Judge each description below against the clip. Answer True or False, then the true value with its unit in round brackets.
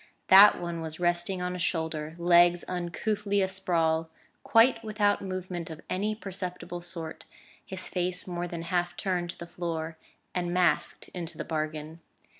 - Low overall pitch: False (175 Hz)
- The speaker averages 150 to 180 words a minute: True (155 wpm)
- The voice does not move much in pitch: True (2.0 semitones)